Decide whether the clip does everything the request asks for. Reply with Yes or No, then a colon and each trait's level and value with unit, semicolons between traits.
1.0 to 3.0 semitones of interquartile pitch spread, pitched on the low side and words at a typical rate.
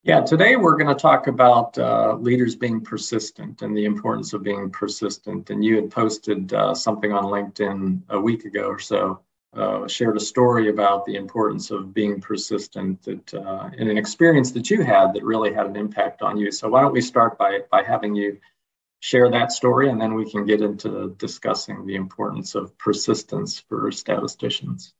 Yes: narrow, 2.6 semitones; low, 105 Hz; average, 190 wpm